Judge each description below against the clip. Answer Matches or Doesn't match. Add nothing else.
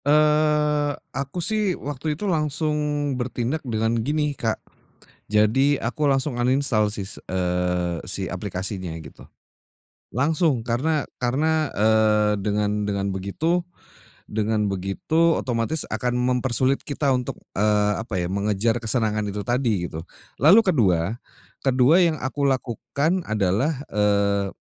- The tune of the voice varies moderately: Doesn't match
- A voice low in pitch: Matches